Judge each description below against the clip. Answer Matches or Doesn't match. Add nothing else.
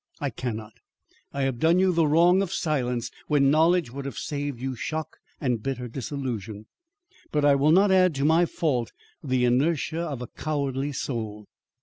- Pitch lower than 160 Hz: Matches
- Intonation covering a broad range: Doesn't match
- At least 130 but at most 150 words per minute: Doesn't match